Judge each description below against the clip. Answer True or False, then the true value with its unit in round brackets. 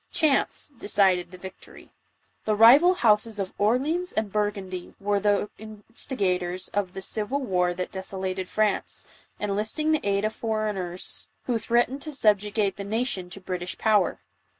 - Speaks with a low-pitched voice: False (205 Hz)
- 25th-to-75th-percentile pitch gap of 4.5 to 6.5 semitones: False (3.1 semitones)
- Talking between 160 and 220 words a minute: False (150 wpm)